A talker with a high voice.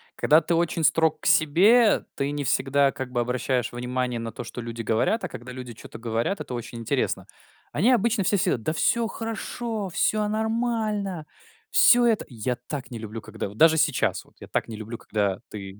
No: medium, 140 Hz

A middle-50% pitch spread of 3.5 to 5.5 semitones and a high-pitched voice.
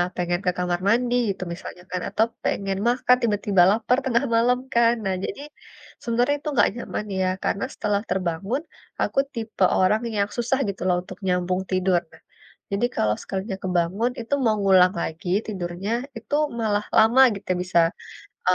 Yes: average, 4.2 semitones; high, 200 Hz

